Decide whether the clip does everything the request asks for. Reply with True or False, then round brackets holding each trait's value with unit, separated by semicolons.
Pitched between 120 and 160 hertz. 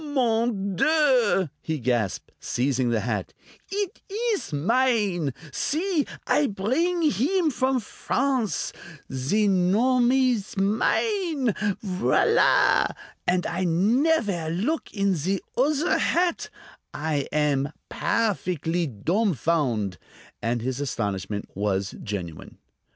False (195 Hz)